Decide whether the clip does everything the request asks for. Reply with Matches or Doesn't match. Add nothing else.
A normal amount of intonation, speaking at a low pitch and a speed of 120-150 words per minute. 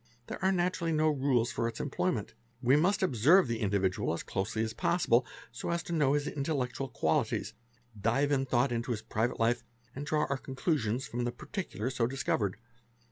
Doesn't match